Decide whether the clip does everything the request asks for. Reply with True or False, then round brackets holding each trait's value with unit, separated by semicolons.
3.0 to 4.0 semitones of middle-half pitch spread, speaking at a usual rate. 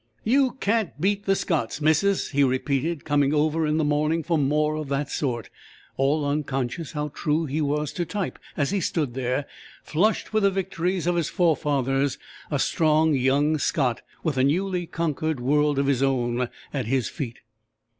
True (3.4 semitones; 175 wpm)